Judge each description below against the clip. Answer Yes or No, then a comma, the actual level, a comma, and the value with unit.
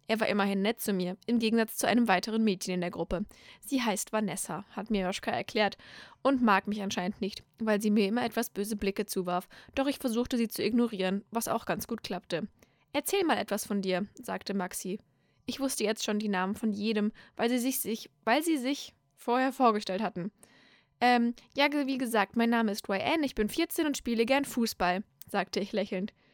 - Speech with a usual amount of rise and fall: Yes, average, 3.6 semitones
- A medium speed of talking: No, fast, 200 wpm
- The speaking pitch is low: No, high, 215 Hz